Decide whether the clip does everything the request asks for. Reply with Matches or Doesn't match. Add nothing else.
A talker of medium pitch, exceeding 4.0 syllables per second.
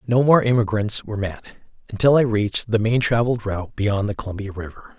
Doesn't match